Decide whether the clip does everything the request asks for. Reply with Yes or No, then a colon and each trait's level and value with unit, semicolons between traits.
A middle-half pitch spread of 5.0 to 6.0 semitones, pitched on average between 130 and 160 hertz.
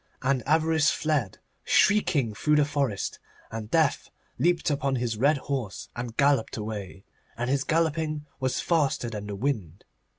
Yes: average, 5.3 semitones; low, 135 Hz